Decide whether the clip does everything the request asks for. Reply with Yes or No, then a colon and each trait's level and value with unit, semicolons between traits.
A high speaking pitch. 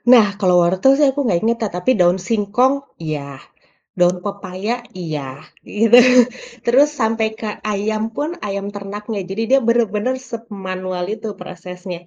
Yes: high, 205 Hz